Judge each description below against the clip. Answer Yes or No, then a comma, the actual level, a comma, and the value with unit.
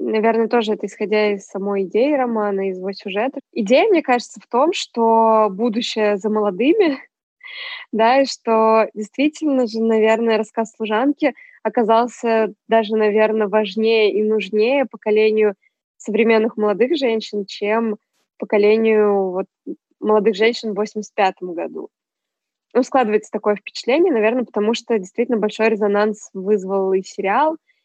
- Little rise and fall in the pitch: Yes, narrow, 2.1 semitones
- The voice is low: No, high, 220 Hz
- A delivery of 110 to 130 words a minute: Yes, average, 125 wpm